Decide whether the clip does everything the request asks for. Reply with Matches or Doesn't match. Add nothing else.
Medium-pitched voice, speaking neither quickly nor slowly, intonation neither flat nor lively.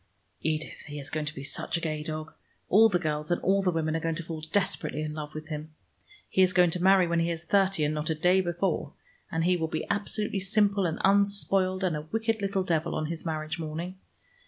Doesn't match